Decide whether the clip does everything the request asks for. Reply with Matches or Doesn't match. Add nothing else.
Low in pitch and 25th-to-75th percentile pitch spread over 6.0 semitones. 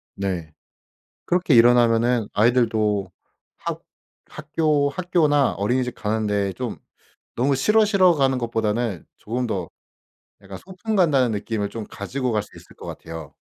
Doesn't match